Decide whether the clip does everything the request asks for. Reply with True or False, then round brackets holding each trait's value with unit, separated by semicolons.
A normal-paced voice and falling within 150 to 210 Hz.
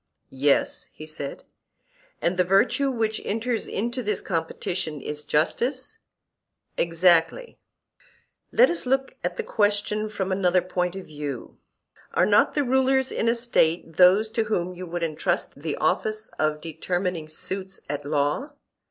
True (145 wpm; 185 Hz)